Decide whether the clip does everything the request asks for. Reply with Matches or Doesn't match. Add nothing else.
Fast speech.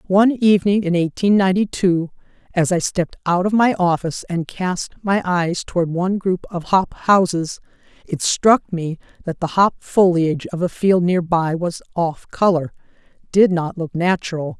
Doesn't match